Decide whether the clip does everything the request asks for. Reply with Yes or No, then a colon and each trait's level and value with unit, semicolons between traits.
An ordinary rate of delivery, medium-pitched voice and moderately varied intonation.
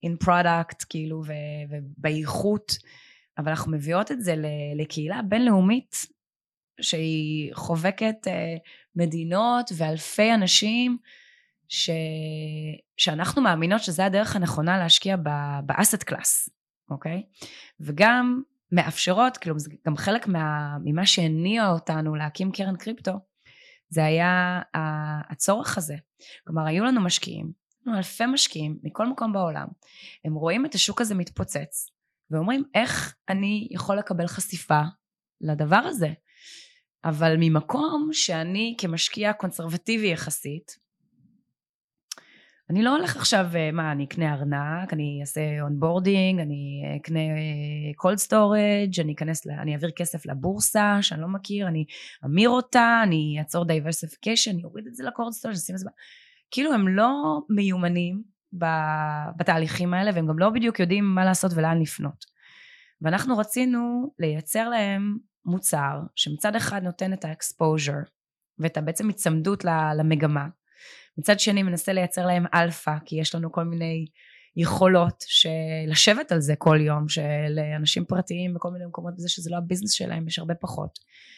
Yes: average, 130 wpm; medium, 175 Hz; average, 4.5 semitones